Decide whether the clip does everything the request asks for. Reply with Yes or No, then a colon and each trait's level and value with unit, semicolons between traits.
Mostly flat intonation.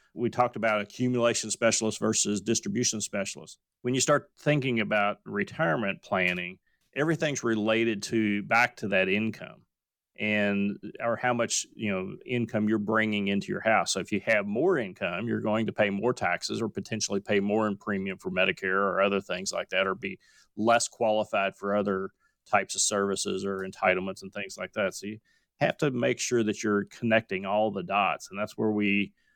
Yes: narrow, 2.2 semitones